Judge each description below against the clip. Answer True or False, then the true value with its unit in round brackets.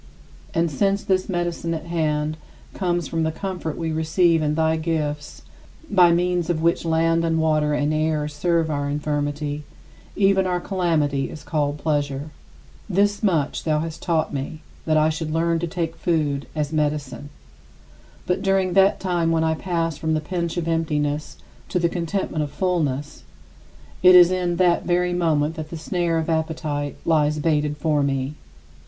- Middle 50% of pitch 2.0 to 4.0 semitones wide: True (2.5 semitones)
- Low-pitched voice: False (160 Hz)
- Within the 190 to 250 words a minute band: False (170 wpm)